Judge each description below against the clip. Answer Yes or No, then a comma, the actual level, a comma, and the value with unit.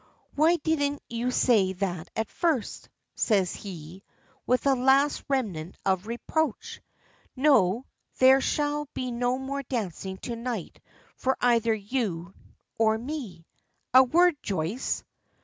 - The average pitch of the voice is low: No, high, 245 Hz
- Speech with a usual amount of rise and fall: No, wide, 5.7 semitones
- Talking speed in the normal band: No, slow, 125 wpm